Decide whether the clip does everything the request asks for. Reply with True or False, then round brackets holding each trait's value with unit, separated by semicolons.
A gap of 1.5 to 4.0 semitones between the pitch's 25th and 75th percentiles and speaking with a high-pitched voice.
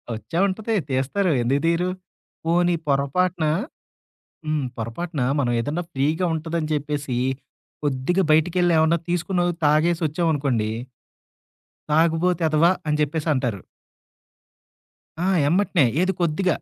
False (3.6 semitones; 160 Hz)